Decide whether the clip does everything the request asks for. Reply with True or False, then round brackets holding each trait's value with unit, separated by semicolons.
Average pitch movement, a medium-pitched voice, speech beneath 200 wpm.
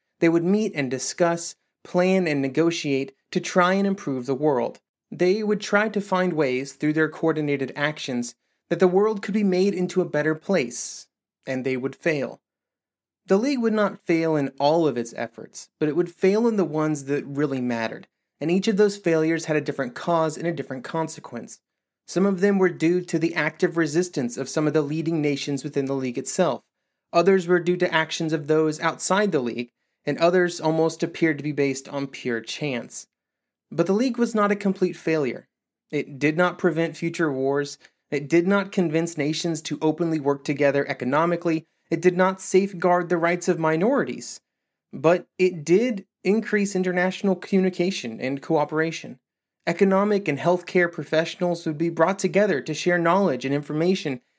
True (3.7 semitones; 165 Hz; 180 wpm)